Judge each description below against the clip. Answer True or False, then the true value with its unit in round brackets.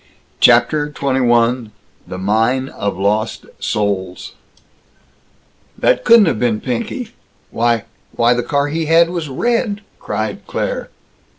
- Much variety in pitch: True (6.9 semitones)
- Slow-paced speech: True (115 wpm)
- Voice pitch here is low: True (130 Hz)